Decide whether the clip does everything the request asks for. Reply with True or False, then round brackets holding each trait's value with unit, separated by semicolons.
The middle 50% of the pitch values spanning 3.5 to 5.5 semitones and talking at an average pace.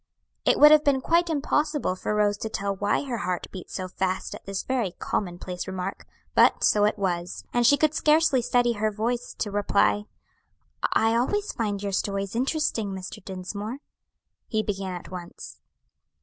True (4.6 semitones; 170 wpm)